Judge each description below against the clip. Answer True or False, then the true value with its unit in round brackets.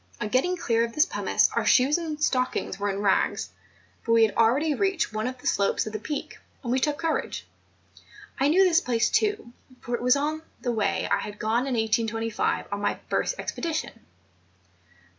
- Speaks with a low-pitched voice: False (250 Hz)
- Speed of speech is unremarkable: True (190 wpm)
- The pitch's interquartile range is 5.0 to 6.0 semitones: True (5.4 semitones)